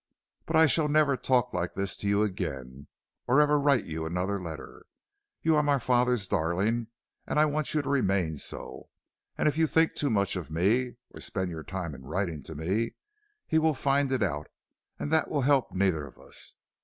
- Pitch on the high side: No, low, 105 Hz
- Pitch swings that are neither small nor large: No, wide, 8.4 semitones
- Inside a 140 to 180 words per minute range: No, average, 200 wpm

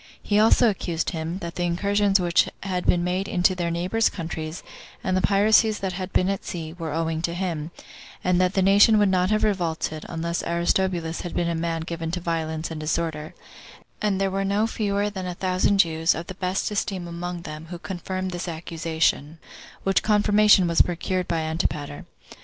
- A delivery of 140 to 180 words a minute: No, average, 190 wpm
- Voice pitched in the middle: Yes, medium, 175 Hz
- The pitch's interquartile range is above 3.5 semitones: No, average, 2.8 semitones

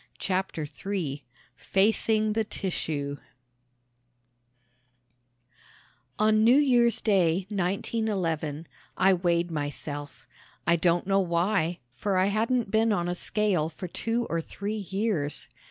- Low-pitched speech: No, high, 190 Hz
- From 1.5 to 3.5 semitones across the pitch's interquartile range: No, average, 4.6 semitones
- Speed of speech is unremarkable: No, slow, 110 wpm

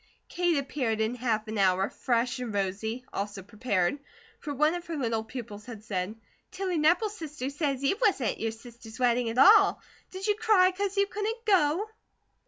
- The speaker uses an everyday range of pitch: No, wide, 8.2 semitones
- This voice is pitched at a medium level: No, very high, 255 Hz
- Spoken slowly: No, average, 185 wpm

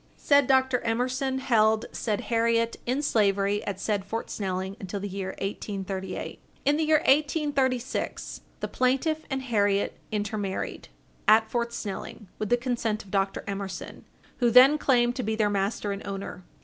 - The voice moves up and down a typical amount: Yes, average, 4.3 semitones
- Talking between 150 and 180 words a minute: Yes, average, 155 wpm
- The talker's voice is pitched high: Yes, high, 220 Hz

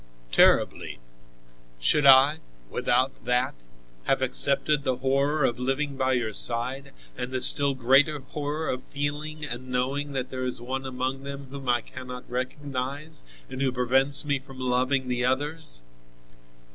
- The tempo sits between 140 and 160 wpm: Yes, average, 145 wpm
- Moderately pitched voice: No, low, 130 Hz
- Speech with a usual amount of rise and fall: No, narrow, 2.0 semitones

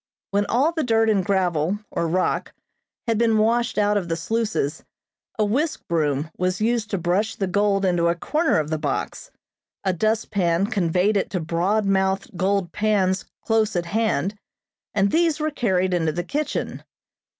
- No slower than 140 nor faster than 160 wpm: No, average, 170 wpm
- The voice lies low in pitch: No, high, 195 Hz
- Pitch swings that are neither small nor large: Yes, average, 4.0 semitones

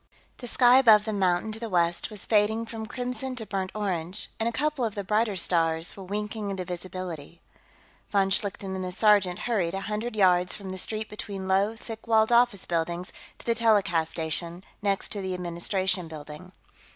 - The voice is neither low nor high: No, high, 195 Hz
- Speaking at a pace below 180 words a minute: No, average, 190 wpm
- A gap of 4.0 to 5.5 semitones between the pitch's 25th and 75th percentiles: No, average, 3.4 semitones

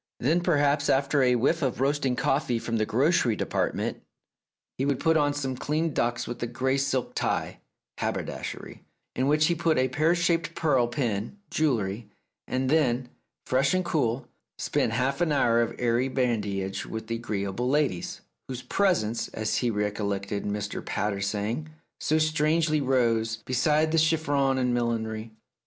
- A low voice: Yes, low, 130 Hz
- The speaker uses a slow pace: No, average, 155 wpm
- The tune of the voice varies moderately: Yes, average, 4.6 semitones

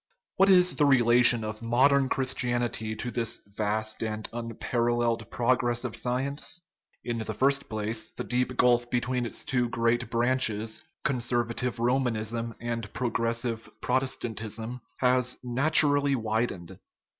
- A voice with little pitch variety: Yes, narrow, 1.9 semitones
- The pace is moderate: No, slow, 125 wpm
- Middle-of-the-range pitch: No, low, 120 Hz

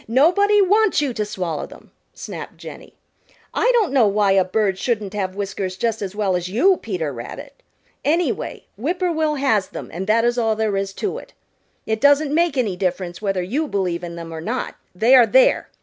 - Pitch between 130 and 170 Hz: No, high, 215 Hz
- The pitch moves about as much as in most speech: No, wide, 7.1 semitones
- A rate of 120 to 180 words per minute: No, average, 200 wpm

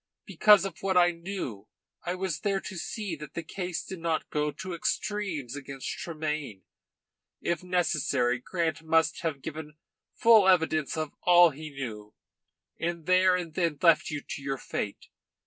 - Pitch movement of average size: Yes, average, 3.6 semitones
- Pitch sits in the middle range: Yes, medium, 165 Hz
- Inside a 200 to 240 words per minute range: No, average, 160 wpm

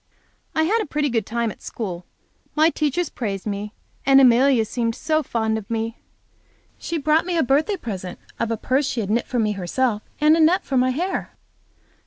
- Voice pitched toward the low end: No, very high, 255 Hz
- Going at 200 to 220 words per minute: Yes, fast, 205 wpm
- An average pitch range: No, wide, 5.7 semitones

